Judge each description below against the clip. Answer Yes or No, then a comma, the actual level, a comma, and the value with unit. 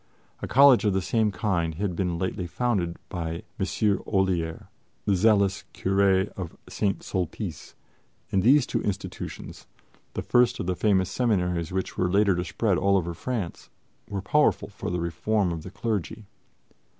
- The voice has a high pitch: No, very low, 95 Hz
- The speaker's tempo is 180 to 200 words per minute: No, average, 160 wpm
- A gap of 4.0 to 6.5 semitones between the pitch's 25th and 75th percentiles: No, average, 3.1 semitones